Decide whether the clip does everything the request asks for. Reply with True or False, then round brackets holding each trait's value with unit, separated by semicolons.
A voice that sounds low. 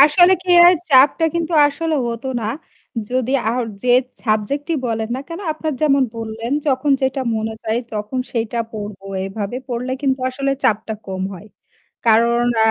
False (245 Hz)